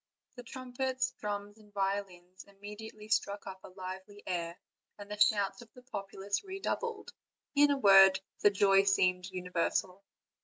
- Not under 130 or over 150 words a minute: Yes, average, 145 wpm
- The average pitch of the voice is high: Yes, high, 200 Hz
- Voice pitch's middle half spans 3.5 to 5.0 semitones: No, narrow, 2.5 semitones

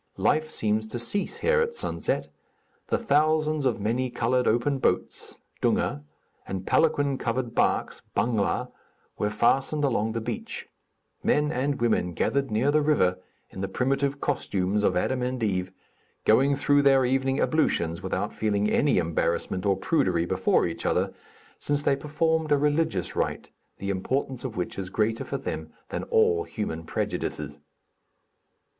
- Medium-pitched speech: No, low, 130 Hz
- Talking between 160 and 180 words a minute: No, average, 150 wpm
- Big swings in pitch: Yes, wide, 5.7 semitones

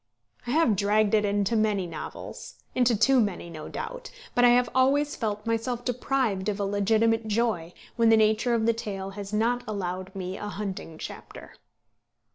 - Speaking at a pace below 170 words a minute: No, average, 175 wpm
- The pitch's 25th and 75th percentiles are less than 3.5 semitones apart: Yes, average, 3.0 semitones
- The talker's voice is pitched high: Yes, high, 215 Hz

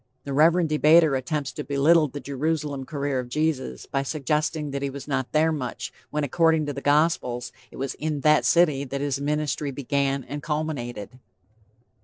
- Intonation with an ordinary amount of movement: No, narrow, 2.0 semitones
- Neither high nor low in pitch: Yes, medium, 145 Hz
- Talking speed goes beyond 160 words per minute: Yes, average, 175 wpm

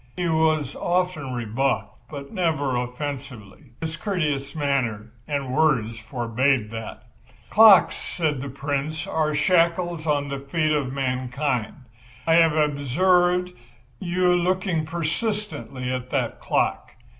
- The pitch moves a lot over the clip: No, average, 4.5 semitones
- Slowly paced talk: Yes, slow, 120 wpm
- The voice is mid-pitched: Yes, medium, 145 Hz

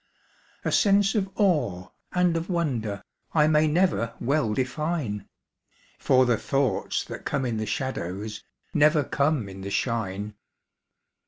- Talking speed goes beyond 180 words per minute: No, slow, 135 wpm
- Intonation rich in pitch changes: Yes, wide, 6.7 semitones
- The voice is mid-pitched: No, low, 130 Hz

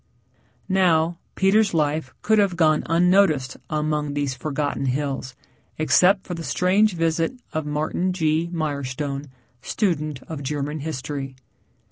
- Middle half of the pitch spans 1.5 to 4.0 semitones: Yes, average, 3.4 semitones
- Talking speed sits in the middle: No, slow, 125 wpm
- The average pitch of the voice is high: No, medium, 155 Hz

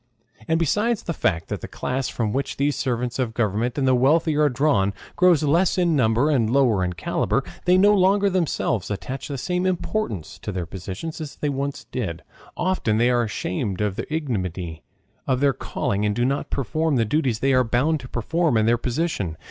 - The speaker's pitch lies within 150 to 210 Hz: No, low, 130 Hz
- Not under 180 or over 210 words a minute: Yes, average, 200 wpm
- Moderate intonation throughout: No, wide, 6.5 semitones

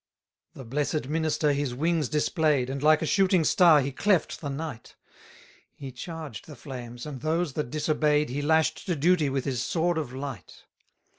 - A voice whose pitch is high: No, medium, 150 Hz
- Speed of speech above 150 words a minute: Yes, average, 175 wpm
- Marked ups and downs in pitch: No, average, 3.0 semitones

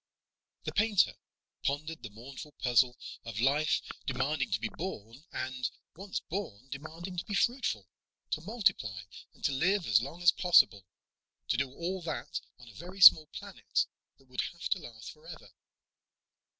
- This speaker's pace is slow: No, average, 155 wpm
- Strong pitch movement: Yes, wide, 6.3 semitones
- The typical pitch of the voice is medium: Yes, medium, 150 Hz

